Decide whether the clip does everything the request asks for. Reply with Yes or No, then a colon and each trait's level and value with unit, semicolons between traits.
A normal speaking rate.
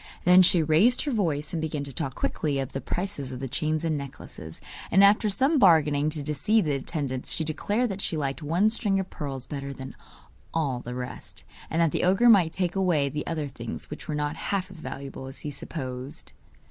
No: fast, 210 wpm